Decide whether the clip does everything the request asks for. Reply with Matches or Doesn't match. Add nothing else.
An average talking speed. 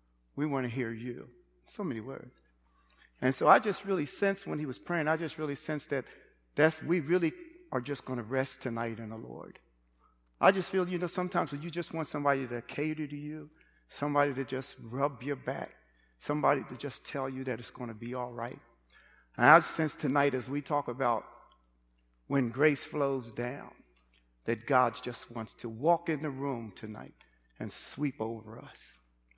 Matches